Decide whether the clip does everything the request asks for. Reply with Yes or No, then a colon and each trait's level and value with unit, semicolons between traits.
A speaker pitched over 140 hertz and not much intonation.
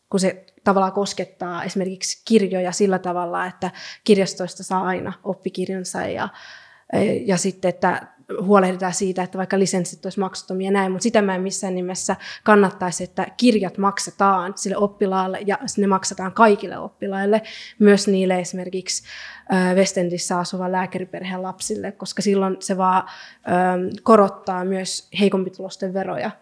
Yes: high, 190 Hz; narrow, 1.2 semitones